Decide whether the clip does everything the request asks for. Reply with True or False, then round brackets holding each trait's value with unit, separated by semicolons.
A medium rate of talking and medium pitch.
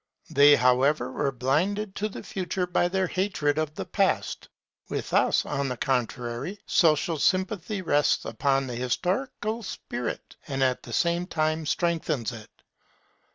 True (145 wpm; 155 Hz)